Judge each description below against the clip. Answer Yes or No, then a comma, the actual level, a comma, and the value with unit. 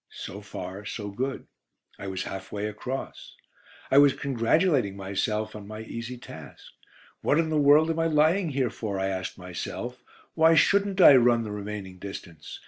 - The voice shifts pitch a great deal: Yes, wide, 6.4 semitones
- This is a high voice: No, low, 115 Hz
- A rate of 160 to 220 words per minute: Yes, average, 170 wpm